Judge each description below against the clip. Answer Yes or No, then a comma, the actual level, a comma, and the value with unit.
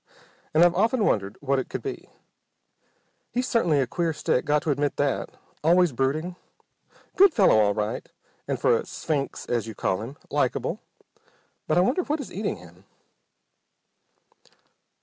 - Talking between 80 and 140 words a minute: No, average, 155 wpm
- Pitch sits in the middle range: Yes, medium, 150 Hz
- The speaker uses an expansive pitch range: Yes, wide, 7.0 semitones